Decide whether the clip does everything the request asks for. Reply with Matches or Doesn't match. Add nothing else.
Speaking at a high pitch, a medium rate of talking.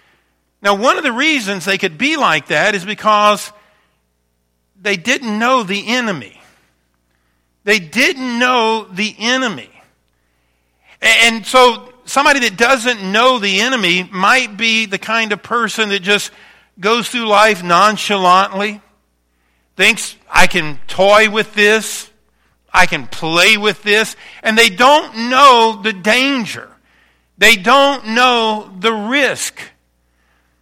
Doesn't match